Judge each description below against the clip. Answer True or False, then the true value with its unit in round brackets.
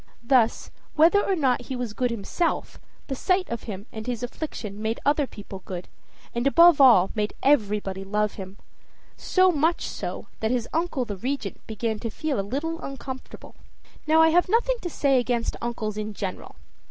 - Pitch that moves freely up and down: True (6.3 semitones)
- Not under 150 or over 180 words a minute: True (175 wpm)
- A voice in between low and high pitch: False (245 Hz)